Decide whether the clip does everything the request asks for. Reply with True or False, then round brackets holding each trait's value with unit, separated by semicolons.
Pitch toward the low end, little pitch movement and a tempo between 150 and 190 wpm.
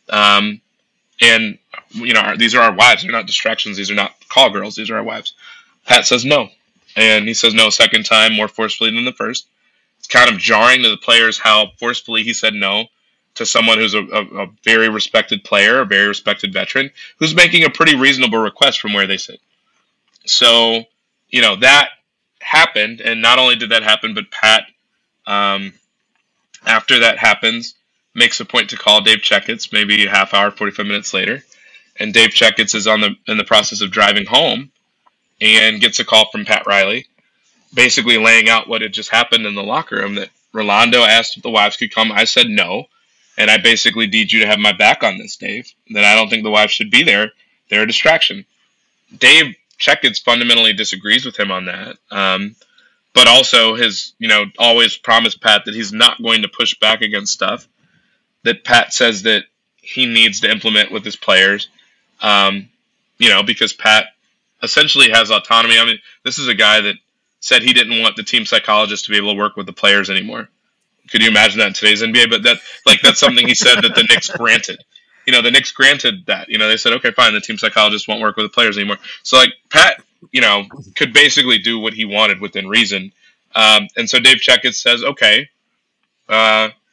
False (110 Hz; 1.6 semitones; 205 wpm)